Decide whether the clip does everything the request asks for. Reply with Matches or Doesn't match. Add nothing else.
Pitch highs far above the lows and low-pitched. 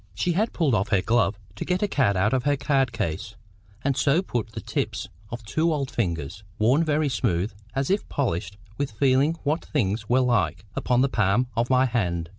Matches